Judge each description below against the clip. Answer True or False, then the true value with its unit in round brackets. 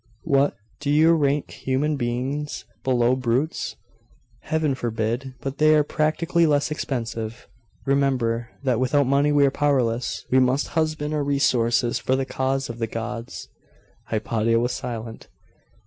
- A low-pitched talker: True (130 Hz)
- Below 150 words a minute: True (140 wpm)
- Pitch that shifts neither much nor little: True (3.5 semitones)